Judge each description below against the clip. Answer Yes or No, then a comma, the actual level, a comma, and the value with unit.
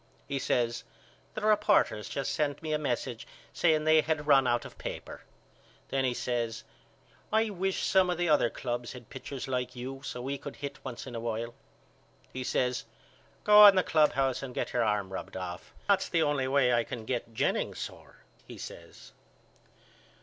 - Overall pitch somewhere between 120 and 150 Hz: Yes, low, 135 Hz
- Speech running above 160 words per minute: Yes, average, 180 wpm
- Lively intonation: No, average, 4.4 semitones